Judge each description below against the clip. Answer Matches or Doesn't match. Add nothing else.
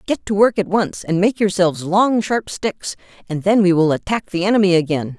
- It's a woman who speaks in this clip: Matches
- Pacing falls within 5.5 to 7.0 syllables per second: Doesn't match